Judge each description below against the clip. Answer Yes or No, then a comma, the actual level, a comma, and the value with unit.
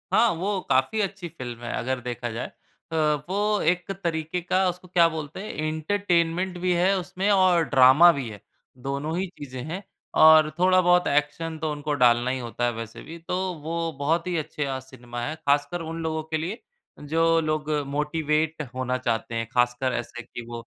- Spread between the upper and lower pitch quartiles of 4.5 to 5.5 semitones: Yes, average, 5.1 semitones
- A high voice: No, medium, 155 Hz